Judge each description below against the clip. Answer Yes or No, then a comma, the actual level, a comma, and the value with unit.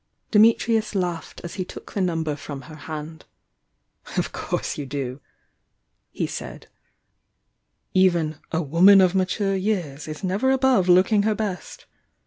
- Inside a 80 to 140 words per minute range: Yes, slow, 135 wpm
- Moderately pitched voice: Yes, medium, 180 Hz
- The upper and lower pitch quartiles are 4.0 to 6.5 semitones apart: Yes, average, 4.4 semitones